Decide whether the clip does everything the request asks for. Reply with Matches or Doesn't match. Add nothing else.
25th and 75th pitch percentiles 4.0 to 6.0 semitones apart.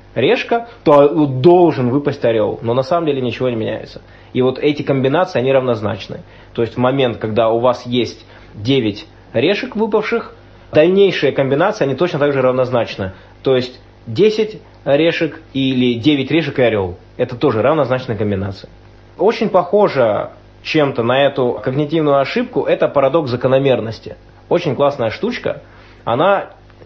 Matches